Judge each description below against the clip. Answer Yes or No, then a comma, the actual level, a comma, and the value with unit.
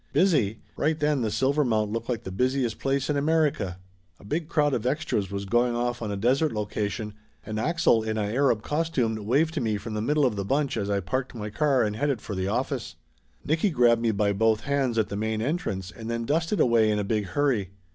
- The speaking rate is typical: No, fast, 225 wpm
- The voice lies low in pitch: Yes, low, 115 Hz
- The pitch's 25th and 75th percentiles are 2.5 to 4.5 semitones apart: No, average, 5.0 semitones